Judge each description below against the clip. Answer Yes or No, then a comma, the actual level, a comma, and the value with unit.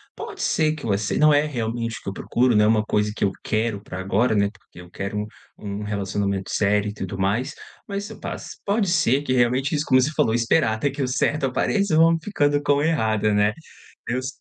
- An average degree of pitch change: No, wide, 5.8 semitones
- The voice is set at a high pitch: No, low, 115 Hz